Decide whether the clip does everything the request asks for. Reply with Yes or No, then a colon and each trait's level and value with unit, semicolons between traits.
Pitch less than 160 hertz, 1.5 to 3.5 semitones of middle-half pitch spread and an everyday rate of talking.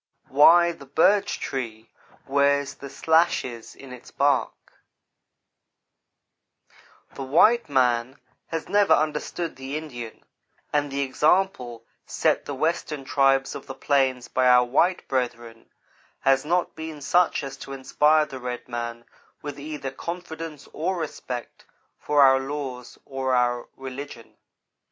No: low, 135 Hz; average, 3.2 semitones; slow, 130 wpm